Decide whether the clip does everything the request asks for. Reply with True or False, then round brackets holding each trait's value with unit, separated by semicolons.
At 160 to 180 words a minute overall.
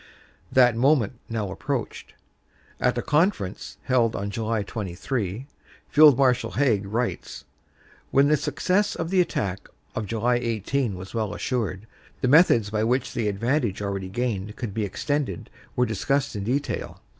False (145 wpm)